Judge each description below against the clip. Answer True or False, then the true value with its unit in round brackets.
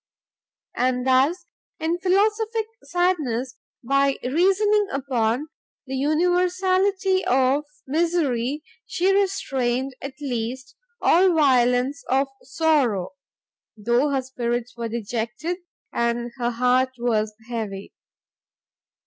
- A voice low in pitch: False (270 Hz)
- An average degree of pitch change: False (6.3 semitones)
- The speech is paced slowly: True (95 wpm)